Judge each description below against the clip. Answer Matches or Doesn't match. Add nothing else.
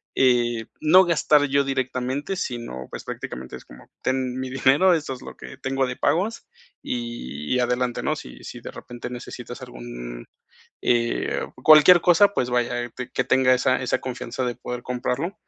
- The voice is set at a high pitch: Doesn't match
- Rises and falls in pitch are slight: Matches